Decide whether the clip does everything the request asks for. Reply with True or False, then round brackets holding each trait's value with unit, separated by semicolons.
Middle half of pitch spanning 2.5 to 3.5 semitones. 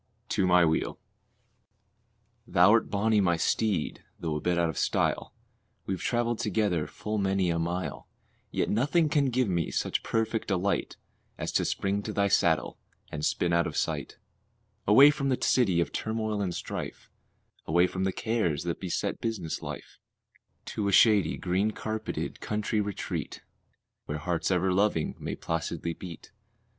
False (4.1 semitones)